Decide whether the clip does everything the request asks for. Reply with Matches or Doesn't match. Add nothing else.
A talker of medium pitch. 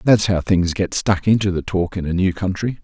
Doesn't match